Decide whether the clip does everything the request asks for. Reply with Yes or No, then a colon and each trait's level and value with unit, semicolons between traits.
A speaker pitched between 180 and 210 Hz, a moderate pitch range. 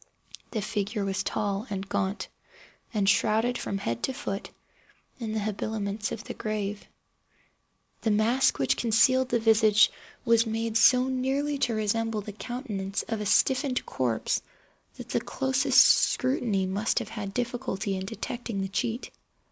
No: high, 220 Hz; average, 3.3 semitones